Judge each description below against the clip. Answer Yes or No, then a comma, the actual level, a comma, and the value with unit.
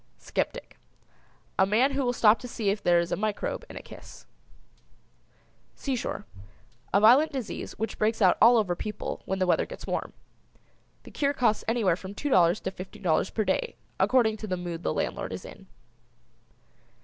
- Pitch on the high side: Yes, high, 215 Hz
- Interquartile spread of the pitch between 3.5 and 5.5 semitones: Yes, average, 4.3 semitones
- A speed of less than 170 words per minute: No, average, 175 wpm